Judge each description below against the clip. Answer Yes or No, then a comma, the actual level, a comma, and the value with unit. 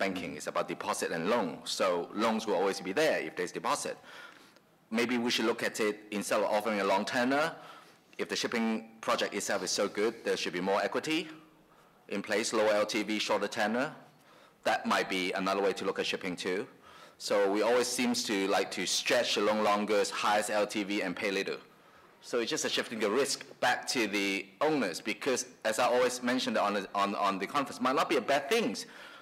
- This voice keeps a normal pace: No, fast, 210 wpm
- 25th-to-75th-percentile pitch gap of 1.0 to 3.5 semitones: Yes, average, 3.0 semitones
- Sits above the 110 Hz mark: No, low, 105 Hz